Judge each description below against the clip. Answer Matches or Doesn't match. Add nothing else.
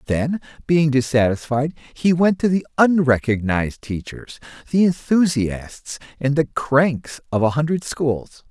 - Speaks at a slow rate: Matches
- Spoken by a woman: Doesn't match